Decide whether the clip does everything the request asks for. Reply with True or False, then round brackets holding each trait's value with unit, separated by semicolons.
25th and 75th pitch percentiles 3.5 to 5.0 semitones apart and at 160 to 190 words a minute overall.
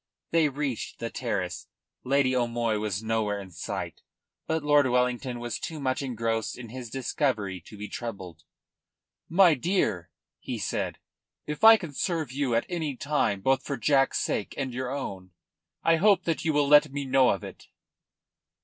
True (4.6 semitones; 165 wpm)